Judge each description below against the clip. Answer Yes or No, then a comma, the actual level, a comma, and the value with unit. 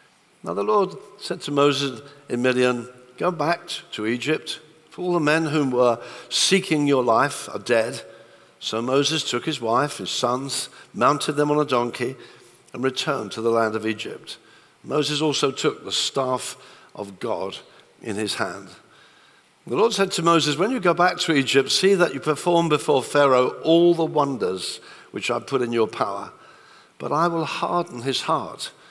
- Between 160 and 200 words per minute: Yes, average, 175 wpm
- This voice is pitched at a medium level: Yes, medium, 145 Hz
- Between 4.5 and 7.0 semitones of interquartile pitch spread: Yes, average, 5.2 semitones